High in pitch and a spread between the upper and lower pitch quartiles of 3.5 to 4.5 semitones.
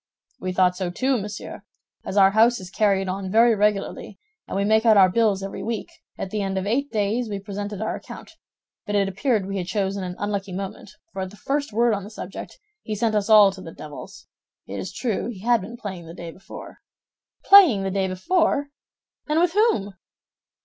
No: high, 205 Hz; average, 2.8 semitones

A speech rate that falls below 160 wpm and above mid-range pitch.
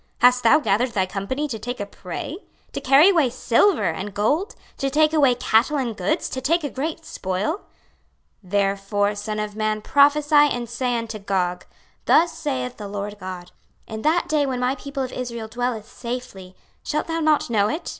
No: average, 185 wpm; high, 245 Hz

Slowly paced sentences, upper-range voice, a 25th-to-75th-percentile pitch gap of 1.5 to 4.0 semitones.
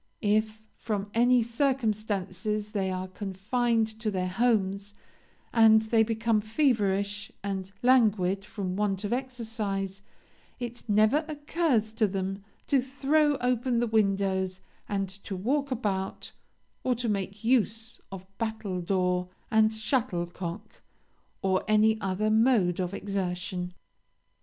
Yes: slow, 120 wpm; high, 215 Hz; average, 3.2 semitones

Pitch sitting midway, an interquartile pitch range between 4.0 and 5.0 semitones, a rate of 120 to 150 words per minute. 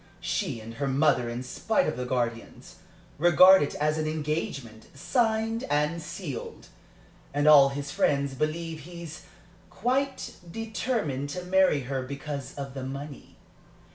Yes: medium, 150 Hz; average, 4.3 semitones; average, 140 wpm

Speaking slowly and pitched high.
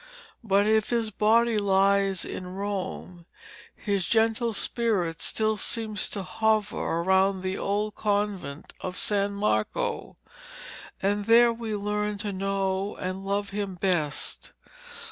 Yes: slow, 125 wpm; high, 200 Hz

